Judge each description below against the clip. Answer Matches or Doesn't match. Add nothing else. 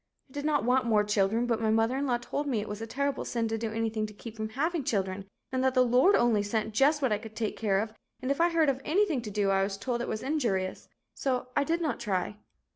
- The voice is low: Doesn't match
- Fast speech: Matches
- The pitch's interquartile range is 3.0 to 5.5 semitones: Matches